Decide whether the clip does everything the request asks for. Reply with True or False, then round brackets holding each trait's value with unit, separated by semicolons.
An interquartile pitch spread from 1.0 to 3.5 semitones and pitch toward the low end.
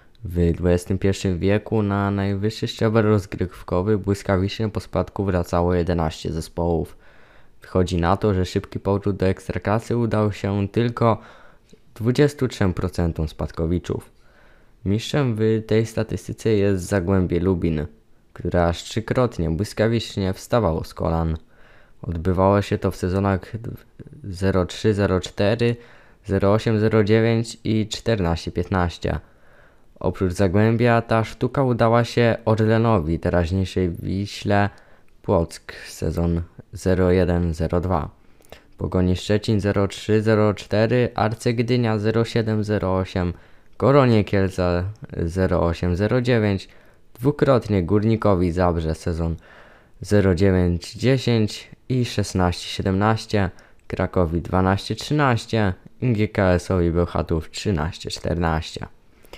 False (3.9 semitones; 100 Hz)